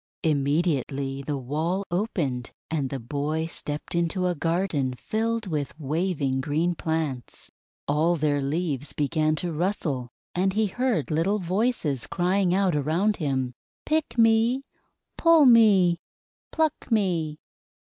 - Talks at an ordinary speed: No, slow, 125 wpm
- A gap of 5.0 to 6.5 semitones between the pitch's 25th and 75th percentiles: Yes, average, 5.3 semitones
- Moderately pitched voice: Yes, medium, 165 Hz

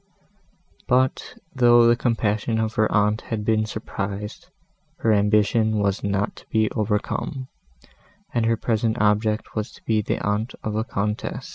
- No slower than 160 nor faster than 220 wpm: No, average, 150 wpm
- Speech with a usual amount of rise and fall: No, narrow, 1.6 semitones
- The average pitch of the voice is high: No, low, 110 Hz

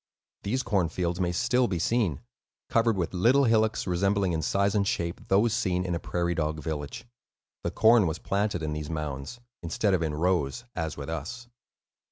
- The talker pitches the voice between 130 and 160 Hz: No, very low, 90 Hz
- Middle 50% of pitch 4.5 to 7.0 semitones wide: Yes, average, 5.1 semitones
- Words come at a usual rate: Yes, average, 185 wpm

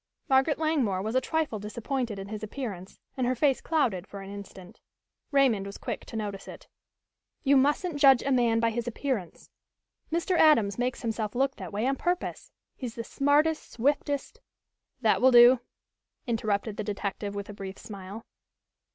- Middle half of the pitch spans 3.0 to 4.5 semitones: No, average, 5.1 semitones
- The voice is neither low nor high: No, high, 235 Hz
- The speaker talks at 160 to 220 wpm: Yes, average, 170 wpm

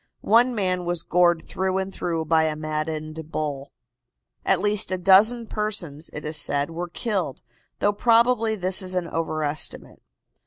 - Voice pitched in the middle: Yes, medium, 175 Hz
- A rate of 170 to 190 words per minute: No, average, 155 wpm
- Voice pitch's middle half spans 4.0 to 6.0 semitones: Yes, average, 4.6 semitones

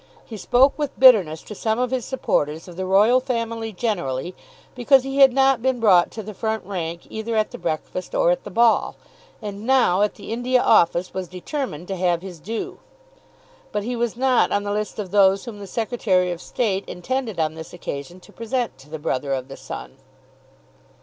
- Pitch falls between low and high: No, high, 210 Hz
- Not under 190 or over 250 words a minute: Yes, average, 200 wpm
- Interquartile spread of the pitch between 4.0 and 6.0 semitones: Yes, wide, 5.5 semitones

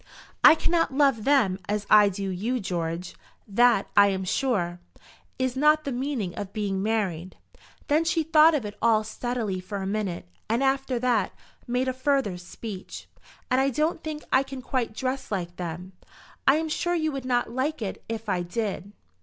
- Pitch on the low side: No, high, 230 Hz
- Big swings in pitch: Yes, wide, 5.7 semitones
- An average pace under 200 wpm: Yes, average, 180 wpm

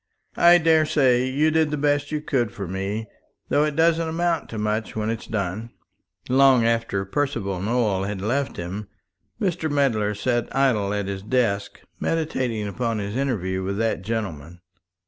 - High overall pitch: No, low, 115 Hz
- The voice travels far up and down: Yes, wide, 6.1 semitones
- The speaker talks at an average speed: Yes, average, 160 wpm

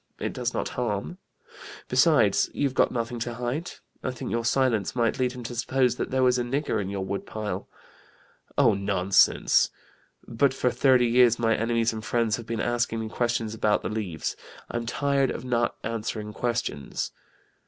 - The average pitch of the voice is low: Yes, low, 120 Hz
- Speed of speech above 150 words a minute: Yes, average, 175 wpm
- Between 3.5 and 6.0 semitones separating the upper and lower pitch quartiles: No, narrow, 2.4 semitones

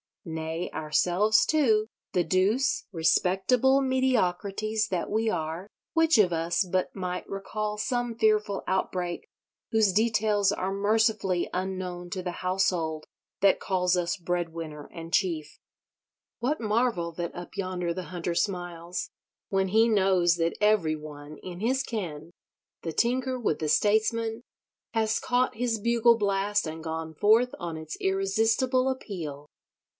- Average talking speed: No, slow, 130 wpm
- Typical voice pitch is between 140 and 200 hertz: Yes, high, 190 Hz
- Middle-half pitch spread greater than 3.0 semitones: Yes, average, 4.2 semitones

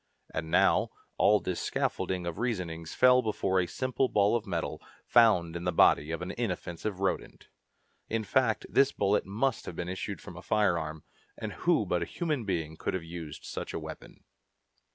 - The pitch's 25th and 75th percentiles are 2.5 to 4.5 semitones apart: No, average, 5.0 semitones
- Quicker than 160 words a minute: Yes, average, 175 wpm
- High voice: No, very low, 95 Hz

